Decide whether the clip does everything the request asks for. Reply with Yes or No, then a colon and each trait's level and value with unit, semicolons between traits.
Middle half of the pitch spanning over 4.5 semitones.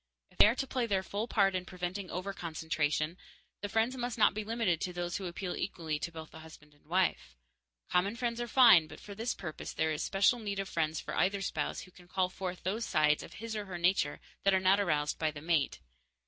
No: average, 4.2 semitones